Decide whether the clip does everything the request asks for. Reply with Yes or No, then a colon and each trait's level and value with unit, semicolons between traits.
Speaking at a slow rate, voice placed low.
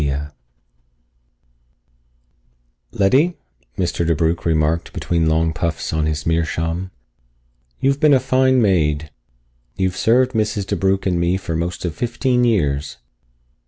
Yes: slow, 120 wpm; very low, 85 Hz